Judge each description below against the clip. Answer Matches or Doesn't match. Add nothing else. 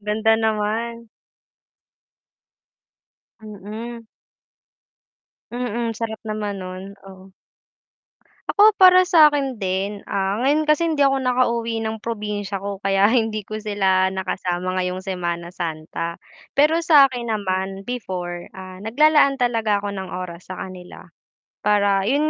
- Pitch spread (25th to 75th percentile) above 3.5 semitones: Matches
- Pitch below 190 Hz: Doesn't match